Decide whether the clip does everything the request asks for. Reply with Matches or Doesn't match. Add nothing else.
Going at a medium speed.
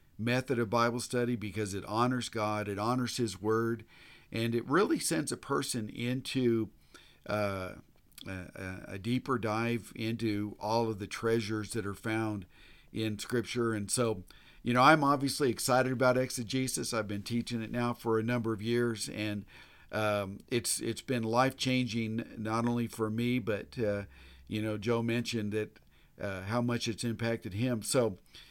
Matches